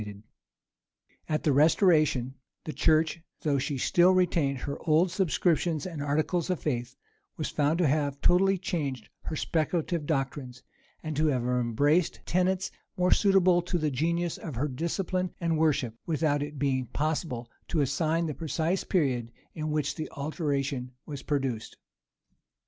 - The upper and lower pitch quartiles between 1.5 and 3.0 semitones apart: No, average, 3.6 semitones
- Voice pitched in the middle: Yes, medium, 155 Hz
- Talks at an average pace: Yes, average, 150 wpm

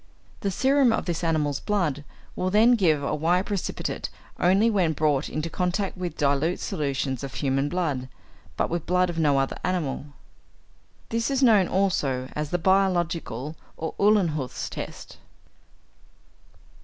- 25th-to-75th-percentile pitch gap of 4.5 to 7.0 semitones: Yes, average, 4.8 semitones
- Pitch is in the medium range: Yes, medium, 170 Hz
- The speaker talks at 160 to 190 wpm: No, average, 145 wpm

